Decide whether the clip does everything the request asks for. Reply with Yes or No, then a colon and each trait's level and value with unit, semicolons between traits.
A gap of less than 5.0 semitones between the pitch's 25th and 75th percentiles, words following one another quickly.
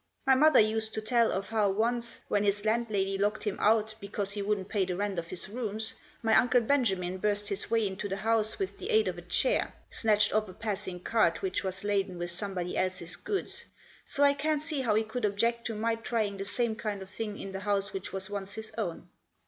Yes: narrow, 2.6 semitones; fast, 230 wpm